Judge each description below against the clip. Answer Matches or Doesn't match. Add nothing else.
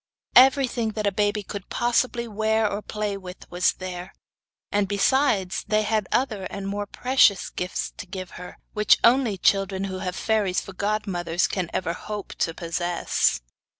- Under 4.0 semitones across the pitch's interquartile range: Matches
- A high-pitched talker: Matches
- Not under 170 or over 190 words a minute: Doesn't match